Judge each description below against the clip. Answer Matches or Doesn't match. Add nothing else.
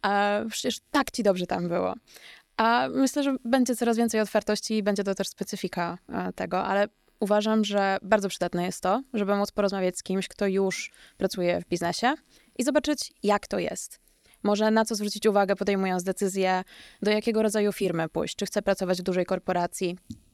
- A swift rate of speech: Matches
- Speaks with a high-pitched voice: Matches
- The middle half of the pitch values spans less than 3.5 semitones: Matches